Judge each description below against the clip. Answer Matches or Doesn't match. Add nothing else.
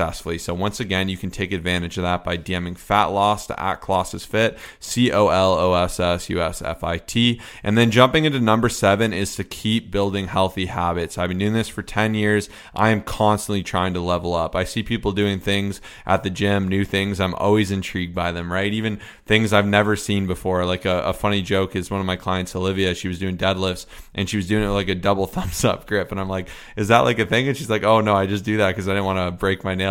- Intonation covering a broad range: Doesn't match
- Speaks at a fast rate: Matches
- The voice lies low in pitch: Matches